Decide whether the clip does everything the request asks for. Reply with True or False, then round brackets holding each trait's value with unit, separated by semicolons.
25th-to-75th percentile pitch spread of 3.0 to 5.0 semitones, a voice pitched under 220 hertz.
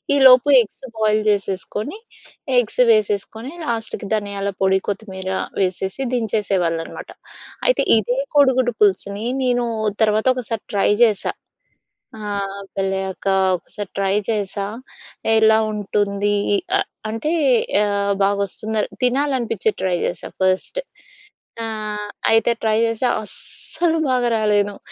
False (2.6 semitones; 210 Hz)